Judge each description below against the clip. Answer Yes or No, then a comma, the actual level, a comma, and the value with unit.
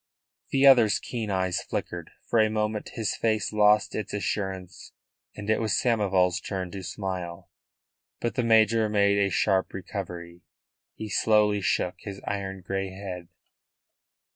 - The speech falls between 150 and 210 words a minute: No, average, 140 wpm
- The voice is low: Yes, low, 100 Hz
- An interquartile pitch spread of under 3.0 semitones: Yes, narrow, 2.5 semitones